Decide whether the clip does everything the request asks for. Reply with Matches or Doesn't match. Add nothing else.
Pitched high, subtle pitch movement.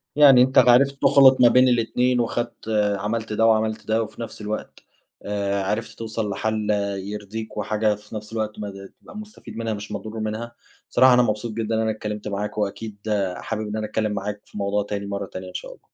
Doesn't match